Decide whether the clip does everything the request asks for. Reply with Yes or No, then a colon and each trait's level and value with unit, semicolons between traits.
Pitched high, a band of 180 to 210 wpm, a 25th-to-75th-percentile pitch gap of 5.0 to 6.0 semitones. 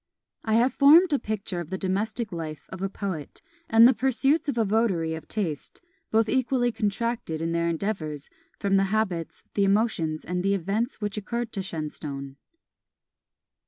No: high, 200 Hz; average, 165 wpm; wide, 5.4 semitones